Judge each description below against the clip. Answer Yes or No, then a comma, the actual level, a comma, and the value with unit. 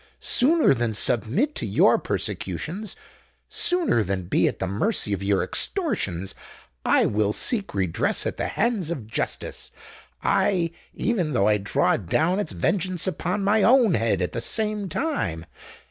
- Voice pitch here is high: No, medium, 155 Hz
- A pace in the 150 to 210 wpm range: No, average, 140 wpm